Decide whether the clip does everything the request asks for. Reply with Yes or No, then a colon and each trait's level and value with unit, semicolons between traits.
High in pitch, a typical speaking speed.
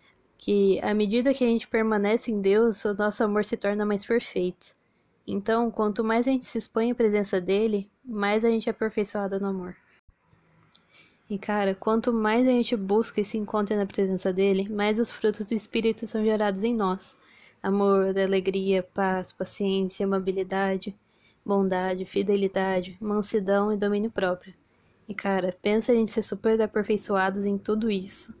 Yes: high, 210 Hz; average, 165 wpm